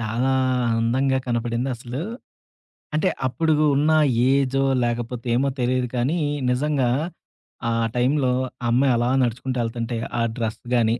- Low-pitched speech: Yes, low, 125 Hz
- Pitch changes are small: Yes, narrow, 2.1 semitones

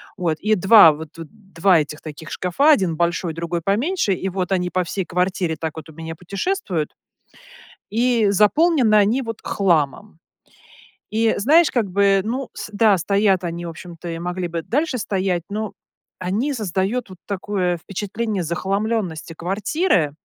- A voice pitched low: No, high, 190 Hz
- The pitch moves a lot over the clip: No, average, 4.2 semitones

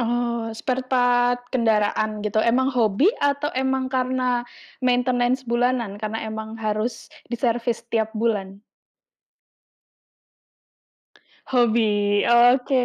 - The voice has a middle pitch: No, high, 240 Hz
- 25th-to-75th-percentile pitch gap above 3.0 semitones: No, narrow, 2.4 semitones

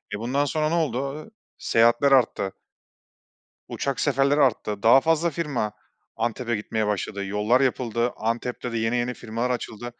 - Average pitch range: Yes, average, 3.5 semitones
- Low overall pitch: Yes, low, 120 Hz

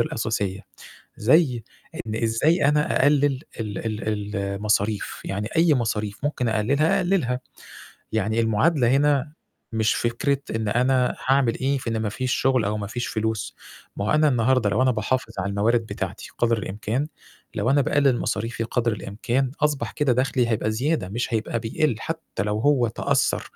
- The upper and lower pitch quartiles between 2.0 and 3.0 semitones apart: No, average, 4.1 semitones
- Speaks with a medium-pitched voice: No, low, 120 Hz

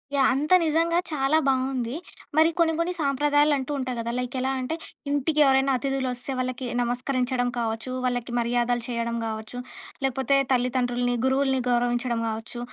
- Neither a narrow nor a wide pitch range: No, narrow, 2.2 semitones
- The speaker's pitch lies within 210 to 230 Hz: No, very high, 255 Hz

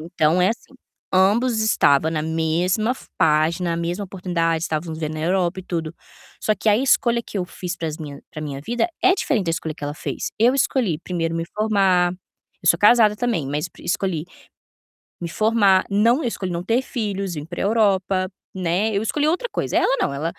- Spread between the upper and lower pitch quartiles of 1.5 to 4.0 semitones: No, average, 4.8 semitones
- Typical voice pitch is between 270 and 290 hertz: No, medium, 185 Hz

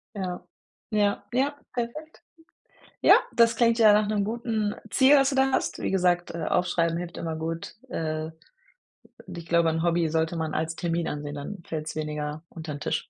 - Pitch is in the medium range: Yes, medium, 175 Hz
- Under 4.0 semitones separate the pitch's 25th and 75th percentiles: No, average, 5.1 semitones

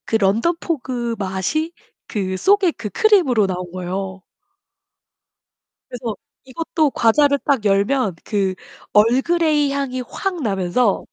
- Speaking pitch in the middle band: No, high, 235 Hz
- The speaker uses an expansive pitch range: Yes, wide, 7.0 semitones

